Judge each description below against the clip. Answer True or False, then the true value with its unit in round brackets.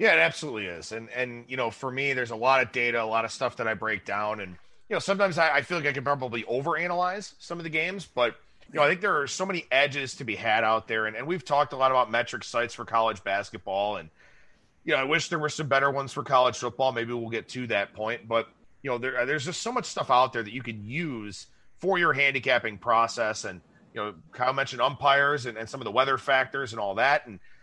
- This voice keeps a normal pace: False (265 wpm)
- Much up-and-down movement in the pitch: False (4.0 semitones)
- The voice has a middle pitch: False (130 Hz)